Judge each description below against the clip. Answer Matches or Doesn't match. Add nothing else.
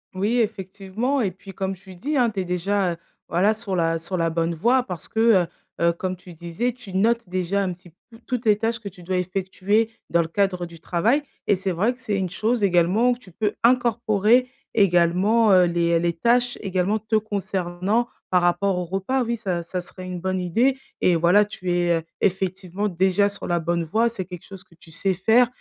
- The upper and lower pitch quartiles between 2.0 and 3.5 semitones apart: Doesn't match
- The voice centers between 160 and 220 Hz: Matches